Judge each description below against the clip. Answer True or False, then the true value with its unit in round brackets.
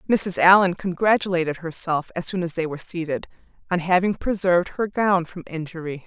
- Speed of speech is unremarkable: True (170 wpm)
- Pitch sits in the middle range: True (175 Hz)